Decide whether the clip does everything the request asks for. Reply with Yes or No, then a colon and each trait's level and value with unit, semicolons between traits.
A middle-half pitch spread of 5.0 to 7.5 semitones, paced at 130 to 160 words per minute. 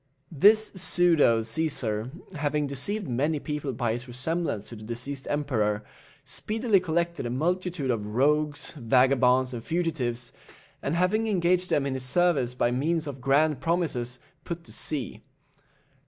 Yes: wide, 5.4 semitones; average, 140 wpm